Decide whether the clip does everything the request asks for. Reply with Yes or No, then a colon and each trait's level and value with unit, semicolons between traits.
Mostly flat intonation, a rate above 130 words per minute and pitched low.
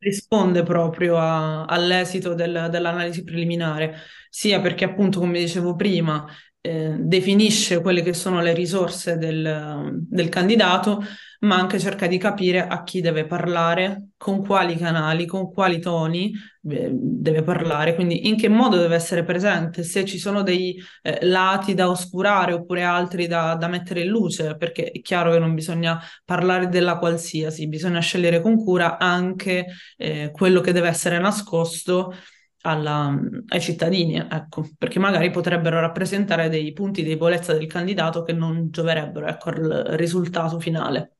No: narrow, 1.9 semitones; average, 150 wpm; medium, 175 Hz